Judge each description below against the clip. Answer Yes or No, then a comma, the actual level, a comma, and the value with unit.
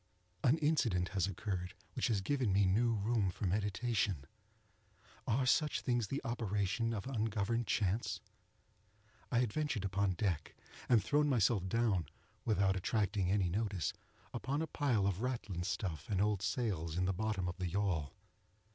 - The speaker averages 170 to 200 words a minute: No, average, 155 wpm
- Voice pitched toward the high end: No, low, 105 Hz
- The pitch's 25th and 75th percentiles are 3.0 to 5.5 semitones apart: Yes, average, 4.1 semitones